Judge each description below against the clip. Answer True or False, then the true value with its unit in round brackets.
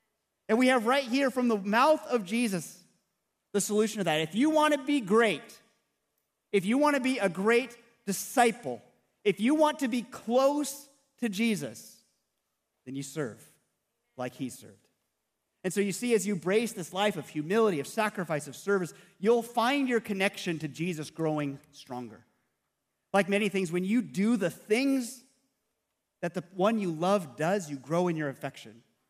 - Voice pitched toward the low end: False (200 Hz)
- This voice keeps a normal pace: True (175 wpm)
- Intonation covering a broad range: True (6.9 semitones)